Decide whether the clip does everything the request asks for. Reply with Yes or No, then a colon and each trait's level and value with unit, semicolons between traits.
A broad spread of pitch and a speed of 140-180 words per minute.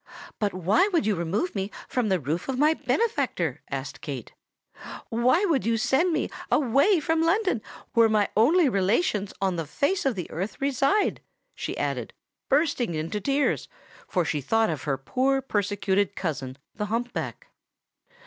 Yes: wide, 7.0 semitones; average, 160 wpm